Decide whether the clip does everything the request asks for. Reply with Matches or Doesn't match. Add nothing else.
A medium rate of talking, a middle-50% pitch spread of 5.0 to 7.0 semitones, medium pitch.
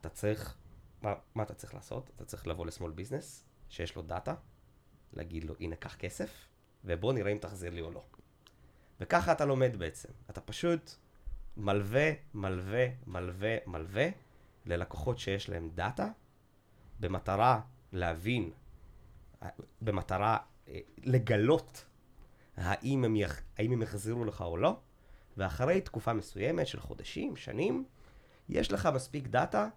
Doesn't match